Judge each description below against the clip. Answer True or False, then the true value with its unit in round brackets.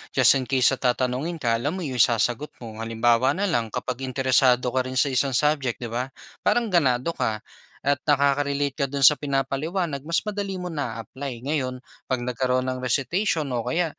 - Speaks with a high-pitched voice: False (135 Hz)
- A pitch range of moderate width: True (3.1 semitones)